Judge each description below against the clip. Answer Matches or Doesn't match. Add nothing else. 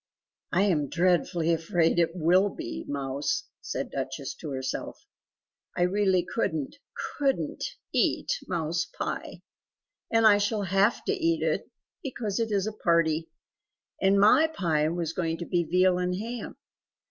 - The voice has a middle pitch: Matches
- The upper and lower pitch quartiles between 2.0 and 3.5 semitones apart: Doesn't match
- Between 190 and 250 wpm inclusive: Doesn't match